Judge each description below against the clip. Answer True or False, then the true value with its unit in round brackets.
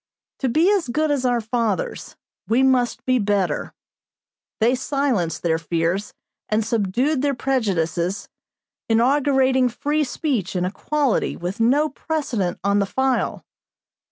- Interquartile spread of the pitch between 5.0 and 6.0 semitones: True (5.5 semitones)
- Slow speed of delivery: True (125 wpm)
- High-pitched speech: True (245 Hz)